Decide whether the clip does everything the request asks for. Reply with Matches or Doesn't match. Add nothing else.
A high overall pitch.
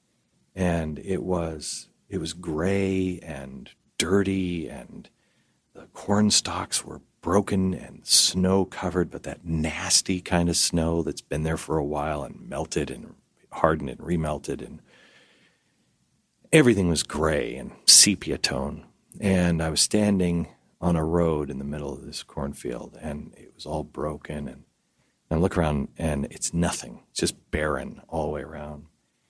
Doesn't match